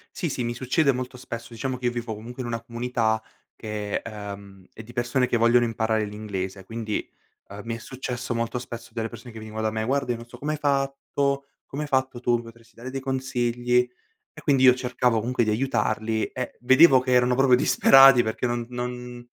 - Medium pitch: No, low, 120 Hz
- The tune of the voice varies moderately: No, narrow, 2.3 semitones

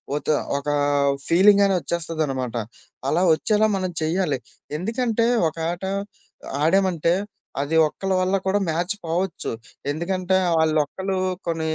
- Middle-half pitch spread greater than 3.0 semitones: Yes, average, 3.4 semitones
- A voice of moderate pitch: Yes, medium, 175 Hz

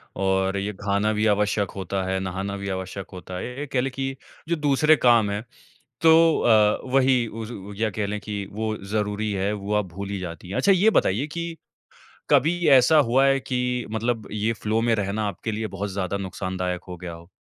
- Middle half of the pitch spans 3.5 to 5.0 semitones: Yes, average, 4.1 semitones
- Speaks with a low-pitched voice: Yes, low, 105 Hz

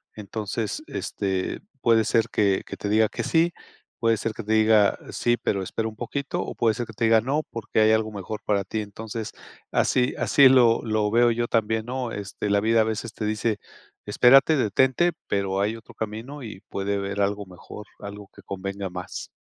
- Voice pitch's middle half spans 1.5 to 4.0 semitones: Yes, narrow, 2.4 semitones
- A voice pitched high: No, low, 110 Hz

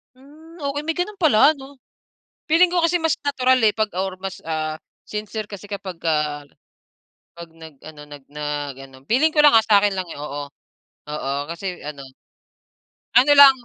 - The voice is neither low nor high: No, high, 205 Hz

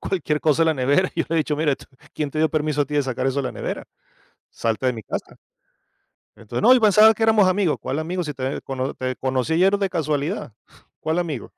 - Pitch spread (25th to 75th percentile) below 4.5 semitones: No, average, 4.8 semitones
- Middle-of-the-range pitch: Yes, medium, 150 Hz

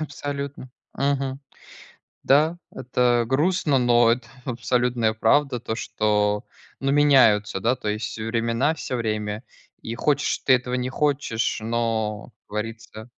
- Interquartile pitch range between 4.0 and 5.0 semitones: No, average, 3.5 semitones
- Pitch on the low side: Yes, low, 120 Hz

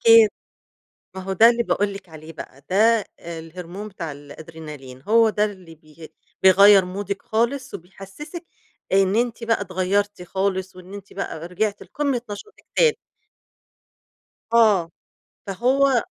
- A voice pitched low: No, high, 195 Hz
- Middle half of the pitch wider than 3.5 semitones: Yes, average, 4.3 semitones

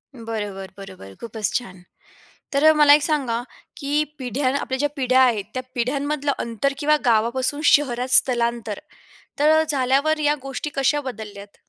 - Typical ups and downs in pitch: Yes, average, 4.0 semitones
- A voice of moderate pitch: No, very high, 255 Hz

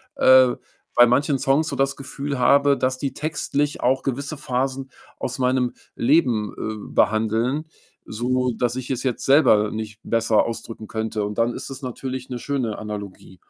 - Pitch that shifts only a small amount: No, average, 3.4 semitones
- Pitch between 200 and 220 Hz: No, low, 125 Hz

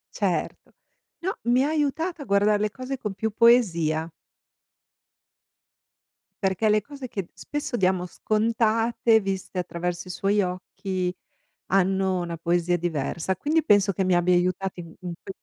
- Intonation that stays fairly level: No, average, 4.2 semitones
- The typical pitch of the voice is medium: No, high, 195 Hz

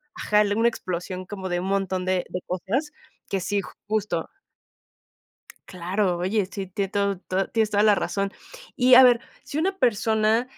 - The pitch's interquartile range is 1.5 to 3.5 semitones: Yes, average, 2.9 semitones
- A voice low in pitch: No, high, 200 Hz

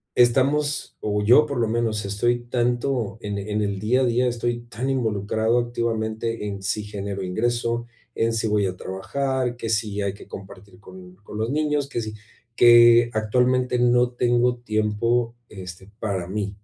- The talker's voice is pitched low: Yes, low, 115 Hz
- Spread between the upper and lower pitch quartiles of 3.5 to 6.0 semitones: No, average, 2.8 semitones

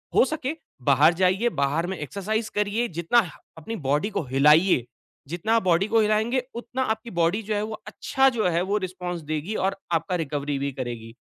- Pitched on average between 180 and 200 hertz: Yes, medium, 185 Hz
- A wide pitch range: Yes, wide, 6.0 semitones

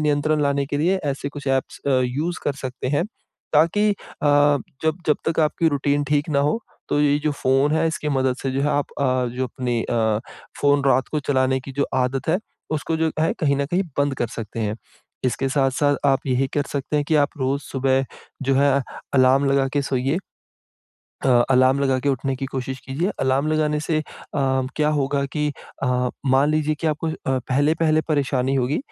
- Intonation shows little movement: Yes, narrow, 2.2 semitones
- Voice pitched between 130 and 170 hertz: Yes, medium, 140 Hz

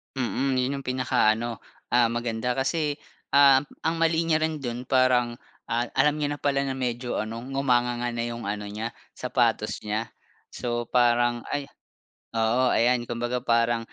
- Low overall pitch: Yes, low, 120 Hz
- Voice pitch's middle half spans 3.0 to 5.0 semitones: No, narrow, 2.5 semitones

